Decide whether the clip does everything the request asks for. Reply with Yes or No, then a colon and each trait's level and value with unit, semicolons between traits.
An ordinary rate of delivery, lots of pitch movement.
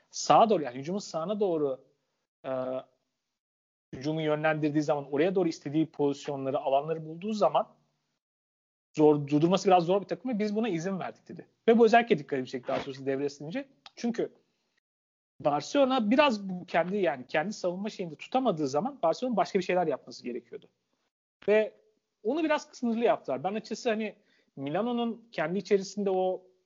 No: fast, 150 wpm; wide, 6.9 semitones